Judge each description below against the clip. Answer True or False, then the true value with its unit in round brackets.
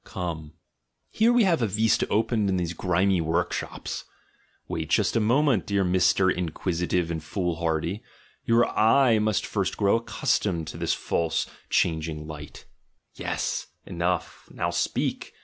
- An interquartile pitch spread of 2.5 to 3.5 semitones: False (4.4 semitones)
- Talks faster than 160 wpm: False (145 wpm)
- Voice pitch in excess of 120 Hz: False (90 Hz)